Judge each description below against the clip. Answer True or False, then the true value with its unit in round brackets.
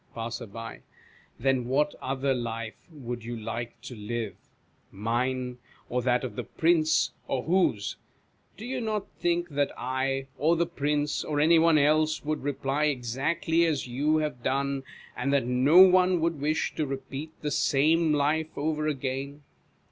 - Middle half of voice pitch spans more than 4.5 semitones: False (3.8 semitones)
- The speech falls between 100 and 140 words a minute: False (155 wpm)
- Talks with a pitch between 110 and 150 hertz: True (140 Hz)